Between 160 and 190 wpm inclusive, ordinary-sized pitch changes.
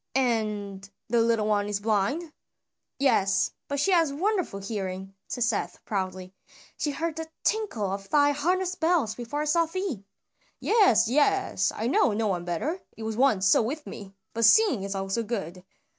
No: average, 170 wpm; wide, 7.6 semitones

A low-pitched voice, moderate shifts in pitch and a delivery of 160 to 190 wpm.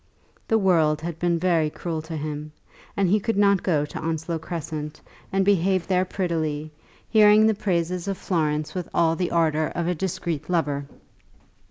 No: medium, 170 Hz; average, 3.2 semitones; average, 170 wpm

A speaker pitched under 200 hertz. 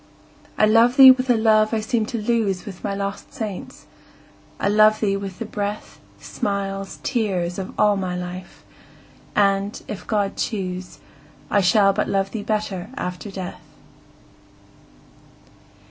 No: high, 205 Hz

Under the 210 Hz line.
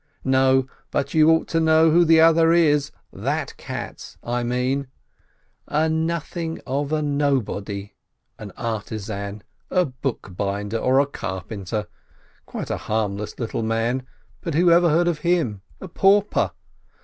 Yes: low, 135 Hz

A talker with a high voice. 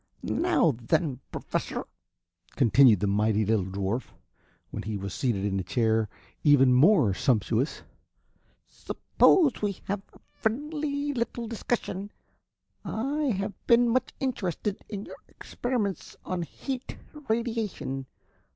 No: medium, 180 Hz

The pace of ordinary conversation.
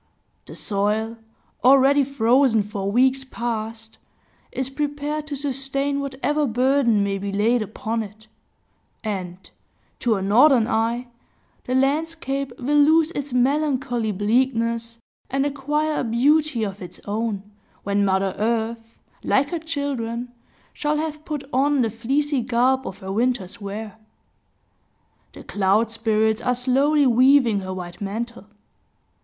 No: slow, 130 wpm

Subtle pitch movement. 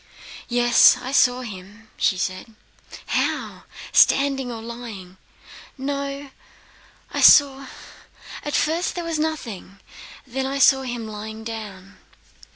No: average, 4.2 semitones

